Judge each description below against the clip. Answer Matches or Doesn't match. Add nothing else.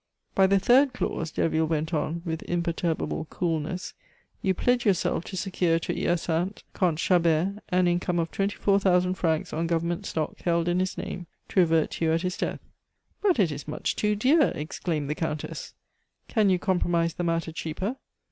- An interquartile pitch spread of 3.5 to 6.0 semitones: Doesn't match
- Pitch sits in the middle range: Matches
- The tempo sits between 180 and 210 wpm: Matches